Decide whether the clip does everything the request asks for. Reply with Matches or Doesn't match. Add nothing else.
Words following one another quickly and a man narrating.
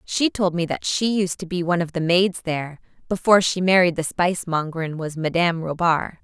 Doesn't match